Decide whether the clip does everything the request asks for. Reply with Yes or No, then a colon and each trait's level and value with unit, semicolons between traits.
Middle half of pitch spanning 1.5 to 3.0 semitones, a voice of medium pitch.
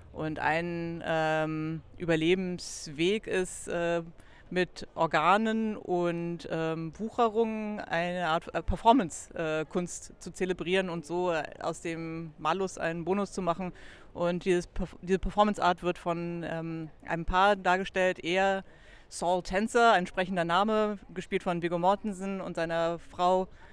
Yes: narrow, 2.5 semitones; medium, 180 Hz